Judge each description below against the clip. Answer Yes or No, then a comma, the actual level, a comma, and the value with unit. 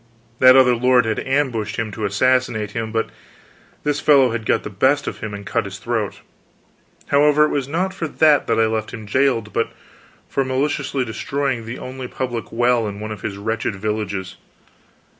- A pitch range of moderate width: Yes, average, 3.6 semitones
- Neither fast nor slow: Yes, average, 185 wpm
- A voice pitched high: No, low, 115 Hz